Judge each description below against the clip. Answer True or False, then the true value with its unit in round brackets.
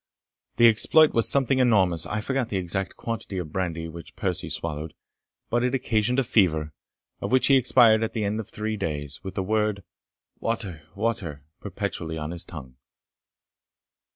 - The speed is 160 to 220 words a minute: True (165 wpm)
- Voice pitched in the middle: False (100 Hz)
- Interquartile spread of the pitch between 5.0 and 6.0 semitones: True (5.6 semitones)